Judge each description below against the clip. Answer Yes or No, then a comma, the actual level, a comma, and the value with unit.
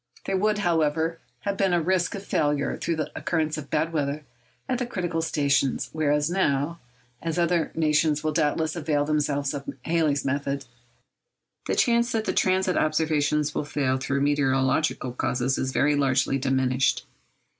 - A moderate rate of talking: Yes, average, 150 wpm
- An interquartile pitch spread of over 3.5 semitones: No, average, 3.2 semitones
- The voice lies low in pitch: No, medium, 150 Hz